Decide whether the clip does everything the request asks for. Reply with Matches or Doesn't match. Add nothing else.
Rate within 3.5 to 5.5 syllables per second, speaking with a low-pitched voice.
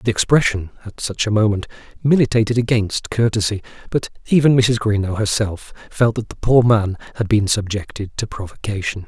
Matches